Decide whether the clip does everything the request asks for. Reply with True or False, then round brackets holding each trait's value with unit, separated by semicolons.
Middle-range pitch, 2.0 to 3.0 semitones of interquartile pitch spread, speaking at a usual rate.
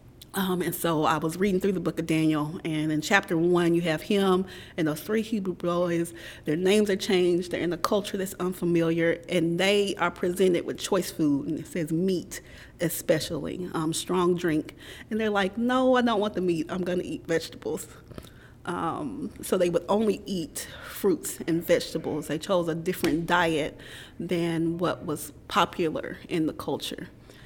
True (175 Hz; 2.7 semitones; 180 wpm)